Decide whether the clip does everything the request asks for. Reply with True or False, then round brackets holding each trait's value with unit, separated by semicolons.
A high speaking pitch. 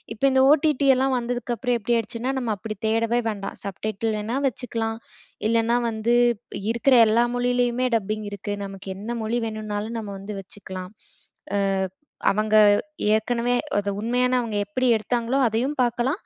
True (230 Hz)